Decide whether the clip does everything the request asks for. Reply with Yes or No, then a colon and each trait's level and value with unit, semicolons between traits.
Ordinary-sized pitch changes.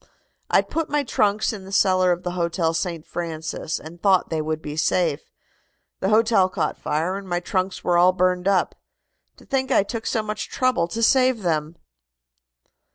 Yes: average, 3.9 semitones